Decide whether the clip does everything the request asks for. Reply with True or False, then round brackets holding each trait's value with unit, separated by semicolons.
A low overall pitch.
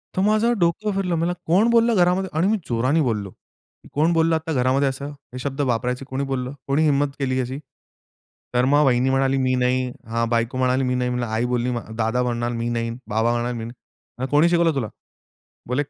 True (130 Hz)